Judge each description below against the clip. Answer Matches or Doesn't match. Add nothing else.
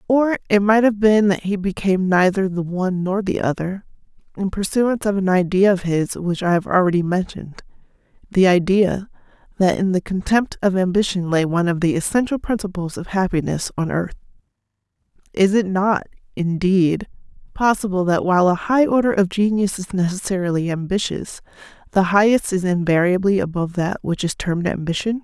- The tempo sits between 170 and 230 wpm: Doesn't match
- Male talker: Doesn't match